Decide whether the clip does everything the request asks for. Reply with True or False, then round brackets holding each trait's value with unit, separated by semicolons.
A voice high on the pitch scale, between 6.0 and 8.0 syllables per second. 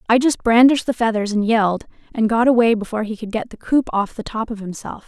True (225 Hz; 6.3 syllables/s)